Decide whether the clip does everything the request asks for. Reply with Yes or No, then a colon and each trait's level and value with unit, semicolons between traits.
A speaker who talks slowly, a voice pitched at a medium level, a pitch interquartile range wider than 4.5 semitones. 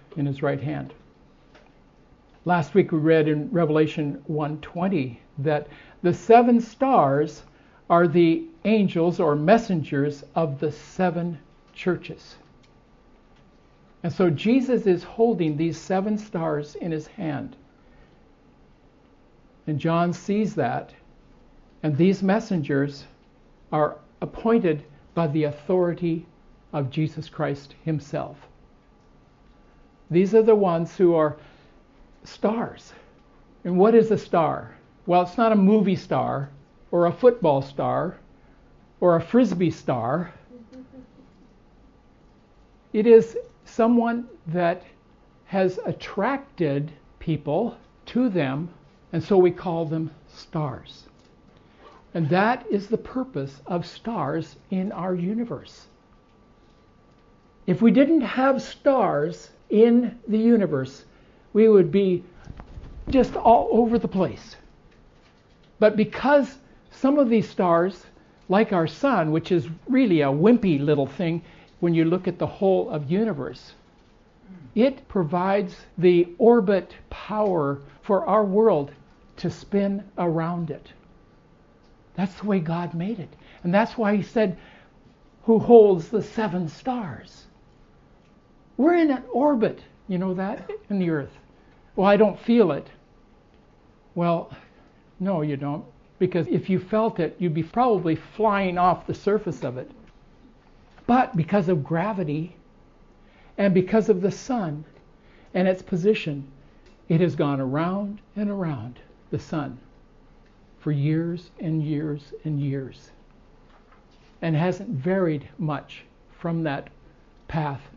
Yes: slow, 120 wpm; medium, 180 Hz; average, 5.3 semitones